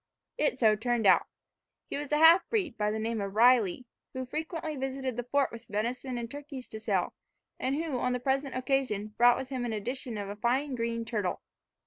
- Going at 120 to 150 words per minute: No, average, 200 wpm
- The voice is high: Yes, very high, 250 Hz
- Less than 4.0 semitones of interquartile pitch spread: Yes, average, 3.5 semitones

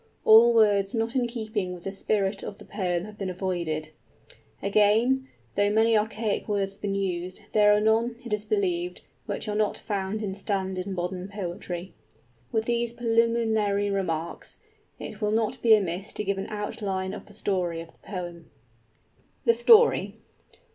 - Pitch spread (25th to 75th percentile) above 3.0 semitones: No, average, 2.7 semitones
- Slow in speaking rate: No, average, 170 wpm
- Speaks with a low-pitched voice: No, high, 205 Hz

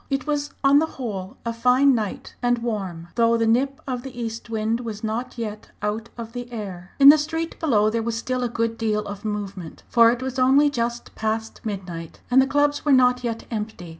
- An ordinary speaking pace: No, fast, 215 wpm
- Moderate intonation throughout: Yes, average, 3.0 semitones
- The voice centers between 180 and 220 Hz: No, high, 230 Hz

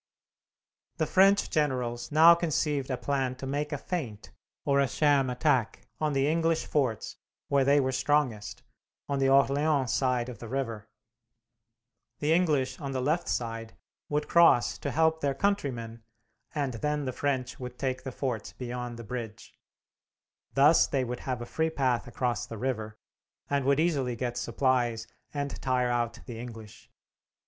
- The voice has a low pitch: Yes, low, 130 Hz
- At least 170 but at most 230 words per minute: No, average, 160 wpm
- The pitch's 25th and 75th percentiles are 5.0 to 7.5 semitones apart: No, average, 3.3 semitones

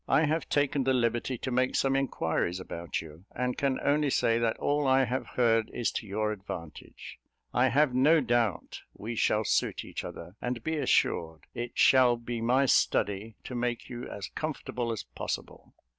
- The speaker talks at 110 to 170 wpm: No, average, 180 wpm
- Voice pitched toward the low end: Yes, low, 120 Hz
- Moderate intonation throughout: Yes, average, 3.5 semitones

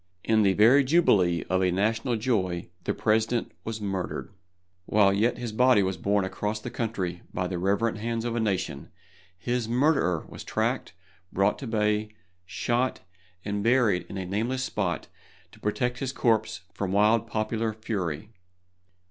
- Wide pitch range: No, average, 3.2 semitones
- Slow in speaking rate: No, average, 155 wpm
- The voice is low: Yes, low, 110 Hz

